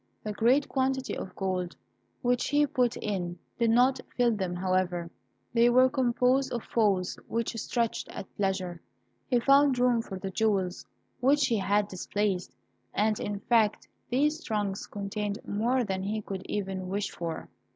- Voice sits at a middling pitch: No, high, 215 Hz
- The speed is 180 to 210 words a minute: No, average, 155 wpm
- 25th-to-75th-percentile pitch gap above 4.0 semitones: Yes, average, 4.4 semitones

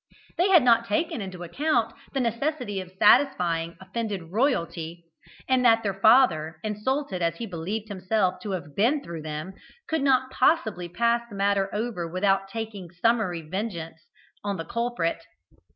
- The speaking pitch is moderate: No, high, 200 Hz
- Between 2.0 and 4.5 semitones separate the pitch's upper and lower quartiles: No, average, 5.2 semitones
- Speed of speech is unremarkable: Yes, average, 150 wpm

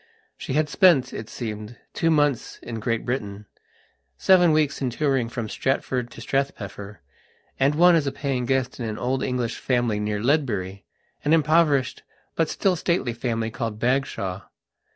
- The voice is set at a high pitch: No, low, 125 Hz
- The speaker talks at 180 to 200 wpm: No, average, 150 wpm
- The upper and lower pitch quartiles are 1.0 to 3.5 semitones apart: No, average, 4.5 semitones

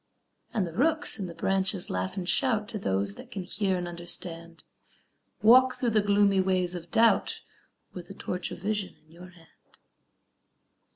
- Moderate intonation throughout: Yes, average, 3.5 semitones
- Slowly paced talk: No, average, 170 wpm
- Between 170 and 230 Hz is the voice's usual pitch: Yes, medium, 185 Hz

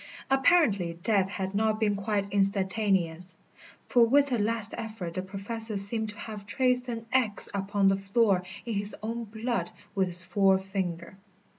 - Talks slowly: No, average, 155 wpm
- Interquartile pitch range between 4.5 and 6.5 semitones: No, average, 2.8 semitones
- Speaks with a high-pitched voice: Yes, high, 205 Hz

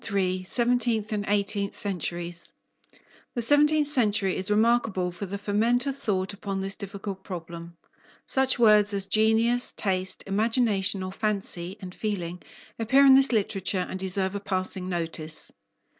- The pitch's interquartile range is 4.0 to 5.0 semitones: No, average, 3.2 semitones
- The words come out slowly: No, average, 145 wpm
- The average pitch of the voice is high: Yes, high, 200 Hz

